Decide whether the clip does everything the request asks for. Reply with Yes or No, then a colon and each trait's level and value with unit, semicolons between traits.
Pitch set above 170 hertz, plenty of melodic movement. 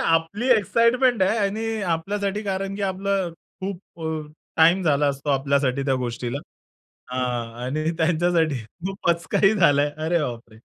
No: medium, 165 Hz; wide, 5.8 semitones